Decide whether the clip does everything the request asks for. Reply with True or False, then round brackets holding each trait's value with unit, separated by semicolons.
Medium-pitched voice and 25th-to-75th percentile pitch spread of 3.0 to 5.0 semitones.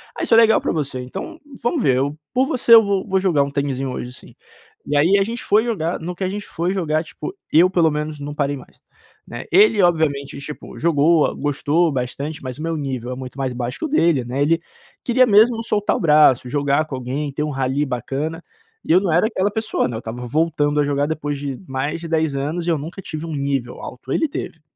True (150 Hz; 4.5 semitones)